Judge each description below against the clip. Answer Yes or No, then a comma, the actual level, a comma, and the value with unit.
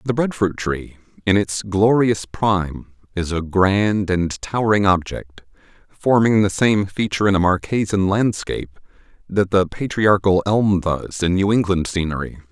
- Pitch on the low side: Yes, low, 100 Hz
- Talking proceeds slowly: No, average, 150 wpm